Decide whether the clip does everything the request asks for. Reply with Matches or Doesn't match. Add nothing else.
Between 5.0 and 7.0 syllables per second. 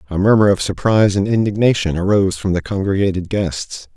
Matches